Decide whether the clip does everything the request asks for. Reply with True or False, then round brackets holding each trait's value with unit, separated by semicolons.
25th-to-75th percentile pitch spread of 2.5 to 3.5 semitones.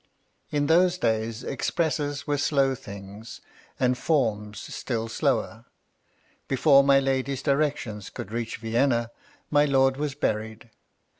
False (4.2 semitones)